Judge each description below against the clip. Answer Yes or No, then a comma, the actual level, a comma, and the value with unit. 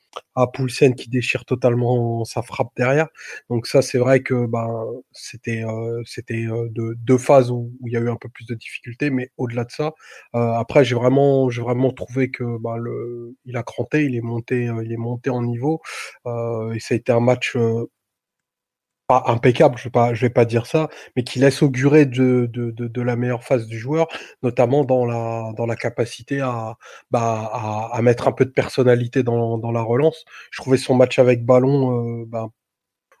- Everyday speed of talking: Yes, average, 210 wpm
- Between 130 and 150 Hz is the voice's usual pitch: No, low, 120 Hz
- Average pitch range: No, narrow, 1.9 semitones